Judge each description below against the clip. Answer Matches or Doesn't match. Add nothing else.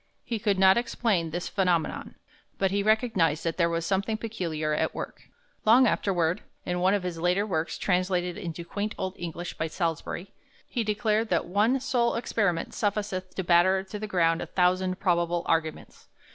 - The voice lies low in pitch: Doesn't match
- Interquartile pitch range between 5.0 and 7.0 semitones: Doesn't match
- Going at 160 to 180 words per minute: Matches